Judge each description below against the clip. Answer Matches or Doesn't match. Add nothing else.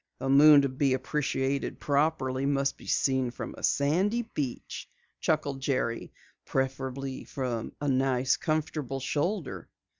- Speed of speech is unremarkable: Doesn't match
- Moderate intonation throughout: Doesn't match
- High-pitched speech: Doesn't match